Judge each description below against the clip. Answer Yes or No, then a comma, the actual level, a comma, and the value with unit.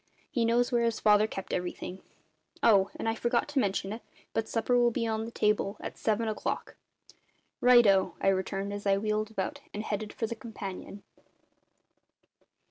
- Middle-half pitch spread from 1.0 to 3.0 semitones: Yes, narrow, 2.6 semitones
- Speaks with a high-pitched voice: Yes, high, 215 Hz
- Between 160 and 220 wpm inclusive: Yes, average, 165 wpm